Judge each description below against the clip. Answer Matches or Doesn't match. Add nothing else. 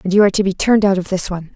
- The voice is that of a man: Doesn't match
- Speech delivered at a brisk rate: Matches